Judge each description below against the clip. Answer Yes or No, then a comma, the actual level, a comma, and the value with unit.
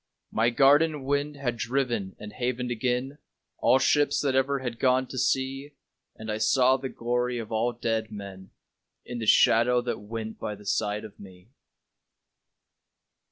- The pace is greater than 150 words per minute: Yes, average, 160 wpm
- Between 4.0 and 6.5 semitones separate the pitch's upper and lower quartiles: No, average, 3.2 semitones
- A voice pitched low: Yes, low, 120 Hz